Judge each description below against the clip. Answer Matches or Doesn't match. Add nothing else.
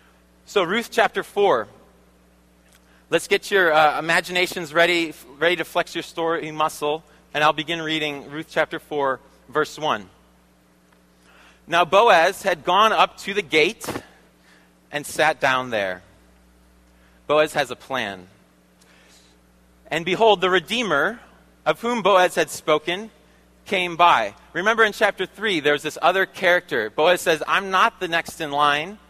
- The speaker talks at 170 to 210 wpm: Doesn't match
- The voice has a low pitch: Doesn't match